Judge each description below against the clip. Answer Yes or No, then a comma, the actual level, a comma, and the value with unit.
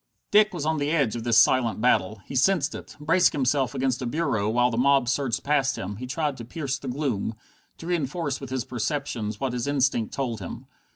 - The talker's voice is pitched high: No, low, 135 Hz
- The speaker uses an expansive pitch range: No, average, 3.6 semitones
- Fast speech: Yes, fast, 215 wpm